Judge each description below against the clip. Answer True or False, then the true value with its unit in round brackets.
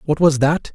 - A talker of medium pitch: True (150 Hz)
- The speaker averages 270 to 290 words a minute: False (245 wpm)